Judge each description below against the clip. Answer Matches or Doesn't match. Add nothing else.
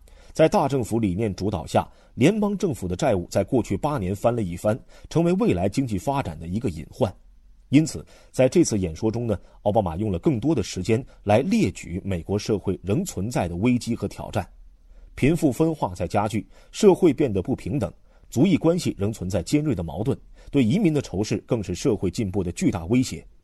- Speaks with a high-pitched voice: Doesn't match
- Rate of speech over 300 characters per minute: Doesn't match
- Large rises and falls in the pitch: Matches